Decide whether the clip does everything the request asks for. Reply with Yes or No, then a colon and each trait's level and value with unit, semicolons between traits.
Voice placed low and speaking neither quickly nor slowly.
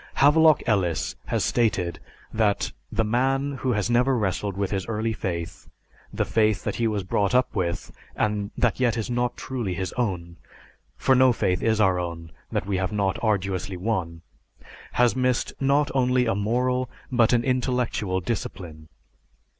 Yes: low, 110 Hz; average, 160 wpm